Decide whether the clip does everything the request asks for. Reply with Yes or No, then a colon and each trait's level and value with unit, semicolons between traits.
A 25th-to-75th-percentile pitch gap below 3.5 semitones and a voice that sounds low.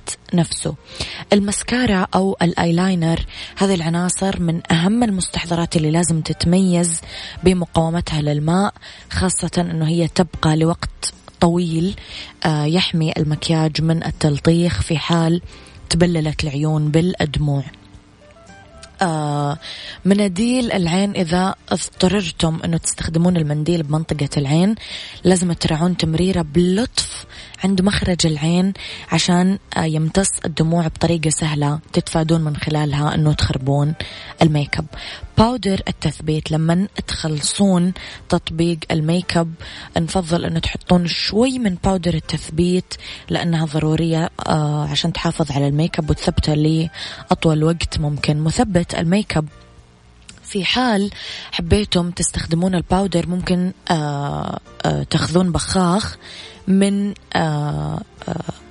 No: average, 2.8 semitones; medium, 170 Hz